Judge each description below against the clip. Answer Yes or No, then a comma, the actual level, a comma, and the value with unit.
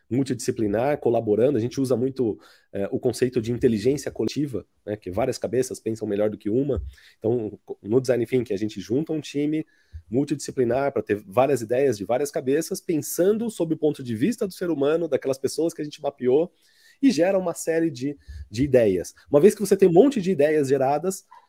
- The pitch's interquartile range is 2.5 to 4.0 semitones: No, average, 5.3 semitones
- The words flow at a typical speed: No, fast, 195 wpm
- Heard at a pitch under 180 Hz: Yes, medium, 140 Hz